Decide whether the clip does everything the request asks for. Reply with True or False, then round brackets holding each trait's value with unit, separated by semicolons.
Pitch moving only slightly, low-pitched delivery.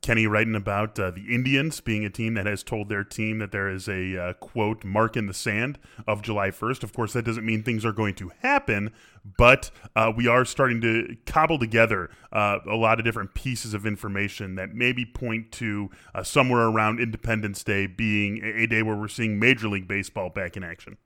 True (2.0 semitones; 110 Hz)